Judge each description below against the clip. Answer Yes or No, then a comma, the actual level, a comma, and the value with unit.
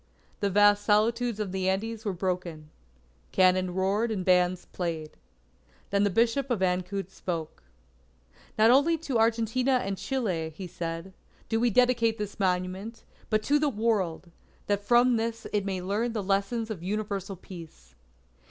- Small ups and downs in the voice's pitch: No, average, 3.8 semitones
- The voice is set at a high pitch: Yes, high, 200 Hz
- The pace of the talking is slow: No, average, 150 wpm